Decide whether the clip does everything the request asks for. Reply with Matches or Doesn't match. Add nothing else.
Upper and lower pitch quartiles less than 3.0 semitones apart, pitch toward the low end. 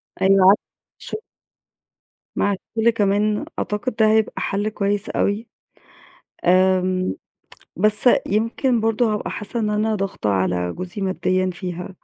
Doesn't match